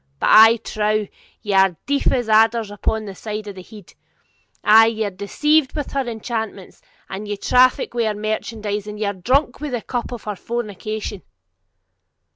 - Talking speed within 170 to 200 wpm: Yes, average, 180 wpm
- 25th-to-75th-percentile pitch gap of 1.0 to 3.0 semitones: Yes, narrow, 2.5 semitones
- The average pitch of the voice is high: Yes, high, 215 Hz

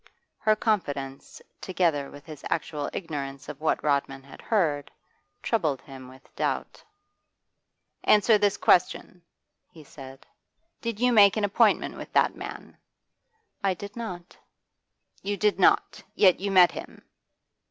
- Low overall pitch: No, medium, 175 Hz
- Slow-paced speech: Yes, slow, 130 wpm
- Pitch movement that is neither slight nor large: No, wide, 6.3 semitones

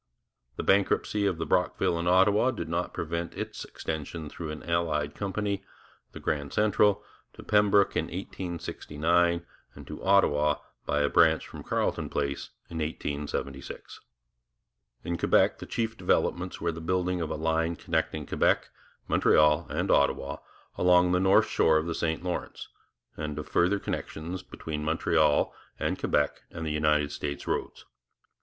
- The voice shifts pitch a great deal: No, average, 3.1 semitones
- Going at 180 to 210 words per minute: No, average, 150 wpm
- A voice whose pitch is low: Yes, very low, 85 Hz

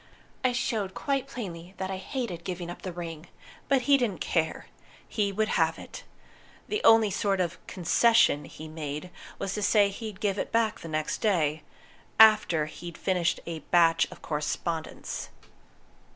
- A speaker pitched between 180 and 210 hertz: Yes, medium, 185 Hz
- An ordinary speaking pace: Yes, average, 155 wpm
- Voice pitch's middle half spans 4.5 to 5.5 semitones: Yes, average, 4.8 semitones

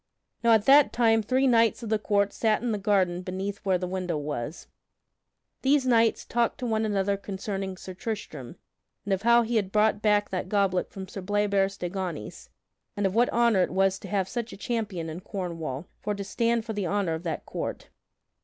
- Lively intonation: No, average, 3.2 semitones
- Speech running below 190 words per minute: No, fast, 205 wpm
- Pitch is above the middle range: Yes, high, 200 Hz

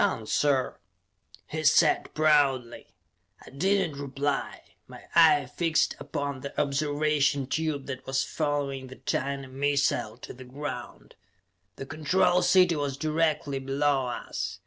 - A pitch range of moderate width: No, narrow, 2.3 semitones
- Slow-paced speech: Yes, slow, 130 wpm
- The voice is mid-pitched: Yes, medium, 145 Hz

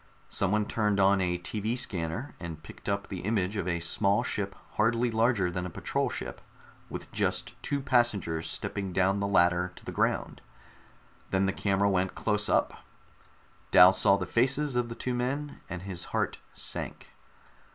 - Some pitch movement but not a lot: Yes, average, 4.0 semitones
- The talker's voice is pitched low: Yes, low, 100 Hz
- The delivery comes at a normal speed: Yes, average, 170 wpm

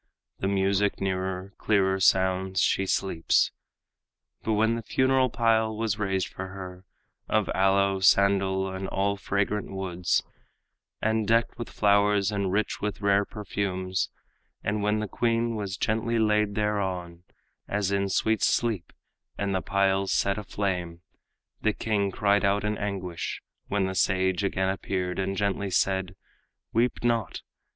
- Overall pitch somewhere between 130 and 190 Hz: No, low, 100 Hz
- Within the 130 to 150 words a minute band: Yes, average, 140 wpm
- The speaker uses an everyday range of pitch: No, narrow, 1.8 semitones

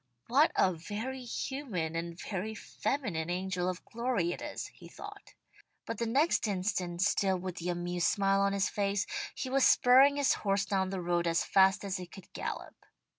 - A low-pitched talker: No, high, 195 Hz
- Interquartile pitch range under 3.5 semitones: No, average, 4.4 semitones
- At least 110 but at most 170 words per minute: No, average, 180 wpm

